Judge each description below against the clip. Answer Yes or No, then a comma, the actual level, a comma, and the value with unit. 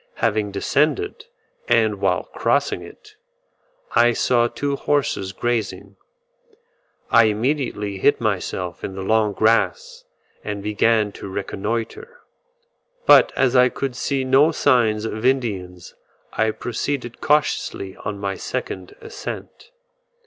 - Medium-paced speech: No, slow, 115 wpm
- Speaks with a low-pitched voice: Yes, low, 115 Hz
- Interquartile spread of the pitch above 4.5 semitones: Yes, average, 5.1 semitones